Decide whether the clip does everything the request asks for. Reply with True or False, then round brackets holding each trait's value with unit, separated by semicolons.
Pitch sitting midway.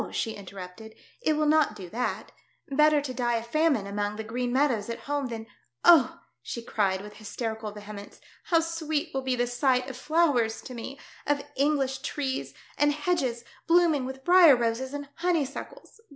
False (260 Hz)